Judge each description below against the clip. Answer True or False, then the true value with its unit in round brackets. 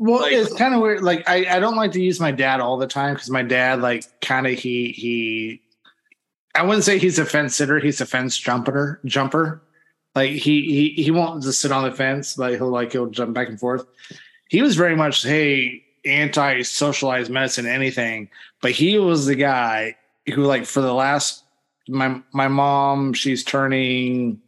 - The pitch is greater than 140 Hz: False (135 Hz)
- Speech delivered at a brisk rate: False (195 wpm)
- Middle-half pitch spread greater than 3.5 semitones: False (2.9 semitones)